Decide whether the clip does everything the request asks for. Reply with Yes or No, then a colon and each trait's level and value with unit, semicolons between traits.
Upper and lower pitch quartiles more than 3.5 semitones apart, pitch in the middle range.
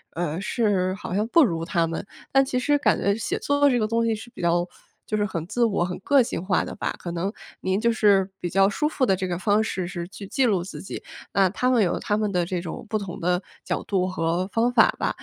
No: average, 4.2 semitones; high, 195 Hz